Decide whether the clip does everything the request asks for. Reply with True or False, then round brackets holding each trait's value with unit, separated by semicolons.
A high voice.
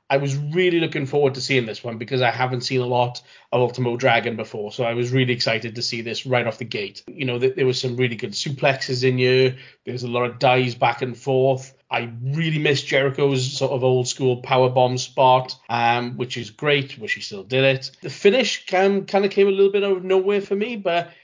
False (130 Hz)